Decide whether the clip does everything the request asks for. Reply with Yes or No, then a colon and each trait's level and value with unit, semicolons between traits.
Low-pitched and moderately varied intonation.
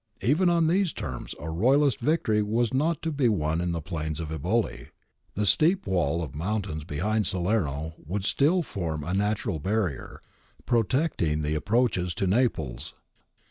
No: low, 100 Hz; wide, 7.3 semitones